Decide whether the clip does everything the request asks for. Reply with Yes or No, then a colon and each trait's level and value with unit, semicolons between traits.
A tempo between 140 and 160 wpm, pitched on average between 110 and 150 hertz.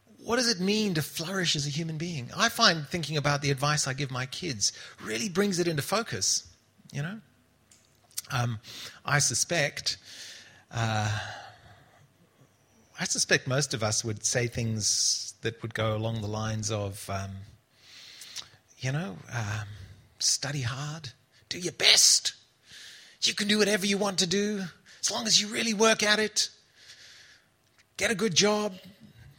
Yes: average, 155 wpm; medium, 140 Hz